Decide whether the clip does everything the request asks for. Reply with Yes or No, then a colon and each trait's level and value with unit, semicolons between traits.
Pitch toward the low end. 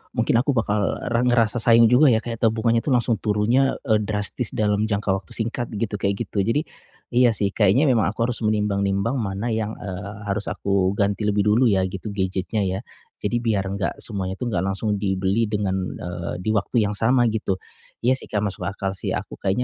Yes: low, 105 Hz